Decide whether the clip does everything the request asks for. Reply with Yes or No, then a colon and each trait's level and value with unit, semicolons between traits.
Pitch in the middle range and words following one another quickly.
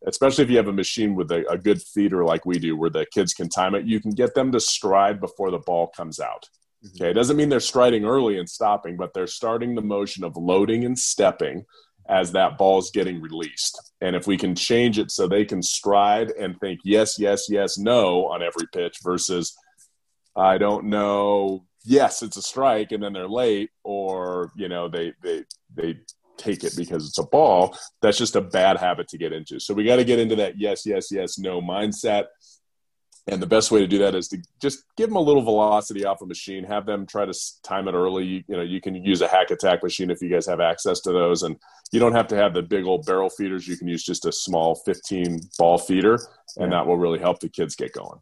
No: low, 100 Hz; fast, 235 wpm